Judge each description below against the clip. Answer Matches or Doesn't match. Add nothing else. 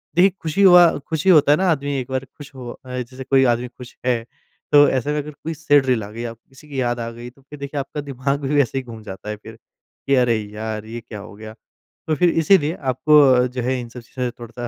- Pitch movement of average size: Matches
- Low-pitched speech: Matches